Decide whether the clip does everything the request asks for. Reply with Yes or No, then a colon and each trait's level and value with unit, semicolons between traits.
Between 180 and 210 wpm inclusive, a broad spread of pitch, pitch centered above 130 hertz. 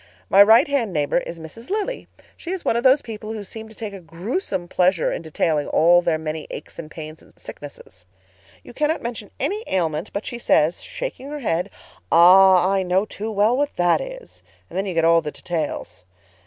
Yes: average, 200 wpm; wide, 6.0 semitones; high, 190 Hz